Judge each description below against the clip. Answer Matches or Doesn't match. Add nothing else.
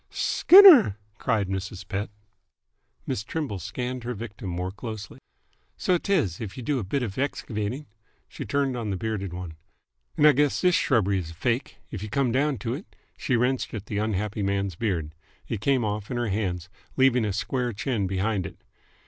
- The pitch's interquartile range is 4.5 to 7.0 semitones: Matches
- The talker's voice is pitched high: Doesn't match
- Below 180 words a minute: Doesn't match